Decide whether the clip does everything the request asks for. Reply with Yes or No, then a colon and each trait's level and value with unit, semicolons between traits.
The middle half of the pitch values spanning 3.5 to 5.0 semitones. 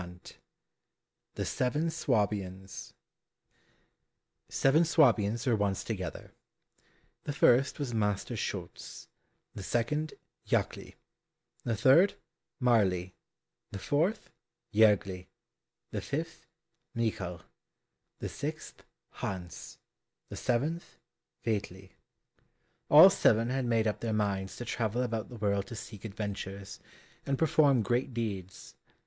Yes: average, 4.6 semitones